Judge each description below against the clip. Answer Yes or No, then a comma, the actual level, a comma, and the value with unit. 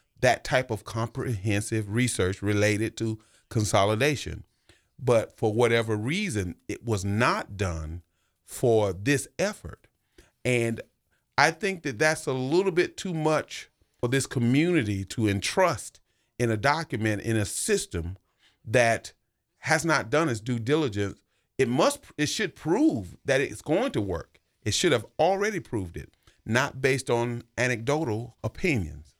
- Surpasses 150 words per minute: No, average, 140 wpm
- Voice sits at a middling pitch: No, low, 120 Hz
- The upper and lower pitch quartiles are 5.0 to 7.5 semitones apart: Yes, wide, 5.5 semitones